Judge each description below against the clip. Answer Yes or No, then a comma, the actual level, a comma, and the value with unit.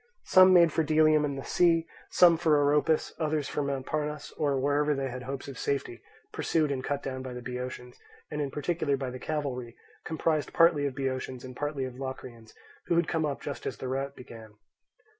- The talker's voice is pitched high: No, medium, 140 Hz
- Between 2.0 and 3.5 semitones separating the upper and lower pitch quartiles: Yes, average, 2.9 semitones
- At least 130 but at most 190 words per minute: No, average, 200 wpm